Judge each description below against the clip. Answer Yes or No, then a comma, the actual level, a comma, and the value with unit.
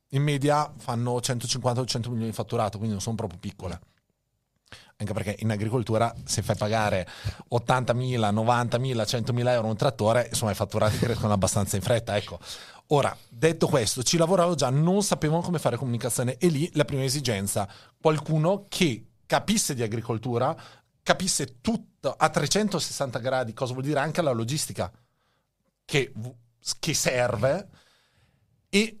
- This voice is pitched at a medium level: No, low, 125 Hz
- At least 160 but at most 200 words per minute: No, average, 145 wpm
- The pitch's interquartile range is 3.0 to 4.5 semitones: No, average, 5.0 semitones